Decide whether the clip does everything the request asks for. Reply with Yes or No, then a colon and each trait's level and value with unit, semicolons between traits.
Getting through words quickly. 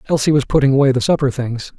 Yes: fast, 235 wpm